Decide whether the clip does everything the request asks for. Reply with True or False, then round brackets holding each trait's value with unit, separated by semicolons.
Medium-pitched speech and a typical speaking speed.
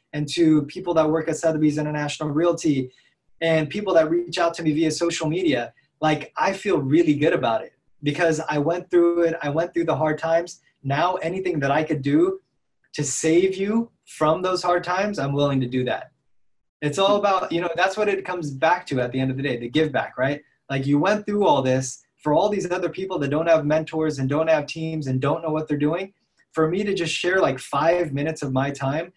False (160 Hz; 230 wpm)